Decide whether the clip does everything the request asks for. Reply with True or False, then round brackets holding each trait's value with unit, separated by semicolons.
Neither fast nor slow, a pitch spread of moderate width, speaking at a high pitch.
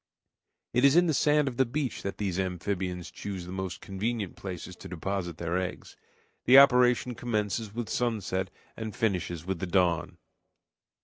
False (165 wpm; 4.8 semitones; 100 Hz)